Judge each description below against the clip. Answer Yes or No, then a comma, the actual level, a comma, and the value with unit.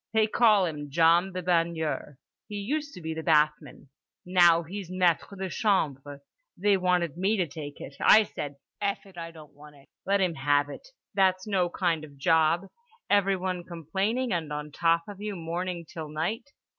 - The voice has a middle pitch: Yes, medium, 175 Hz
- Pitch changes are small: No, average, 3.7 semitones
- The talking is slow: No, average, 180 wpm